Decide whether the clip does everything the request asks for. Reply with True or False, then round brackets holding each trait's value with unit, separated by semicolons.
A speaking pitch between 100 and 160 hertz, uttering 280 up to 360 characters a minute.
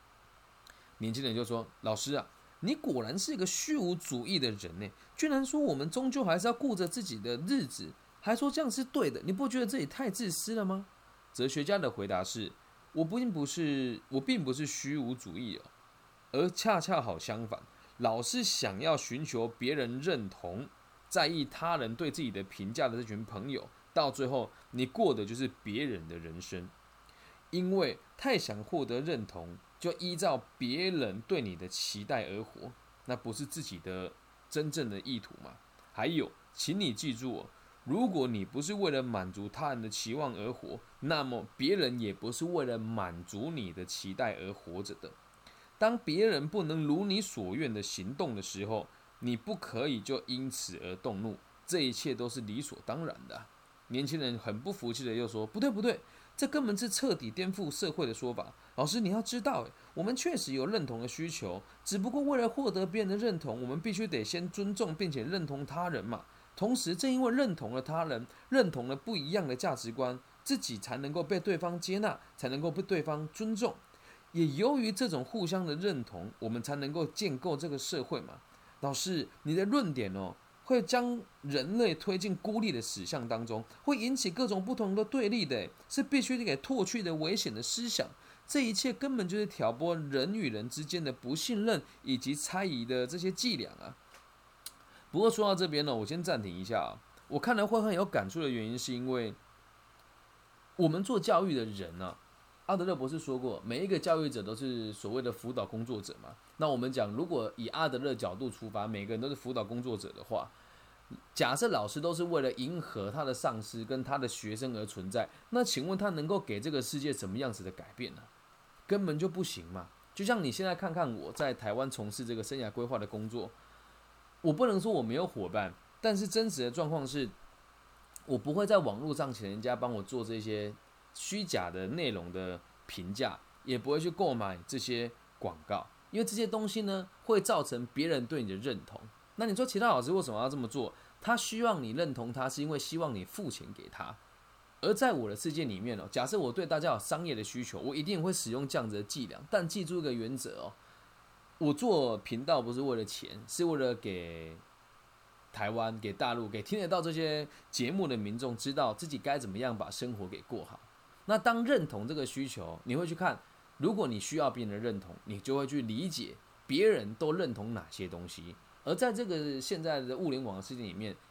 True (140 Hz; 290 characters per minute)